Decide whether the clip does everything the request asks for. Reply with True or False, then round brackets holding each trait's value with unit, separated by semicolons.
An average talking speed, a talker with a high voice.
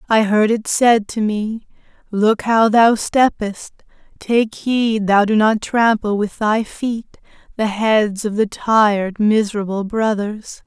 True (145 wpm; 215 Hz)